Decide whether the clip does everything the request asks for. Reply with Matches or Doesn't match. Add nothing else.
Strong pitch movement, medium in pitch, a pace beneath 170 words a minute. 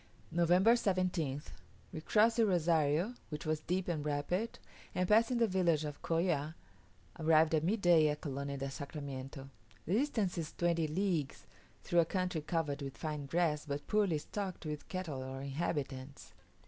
Doesn't match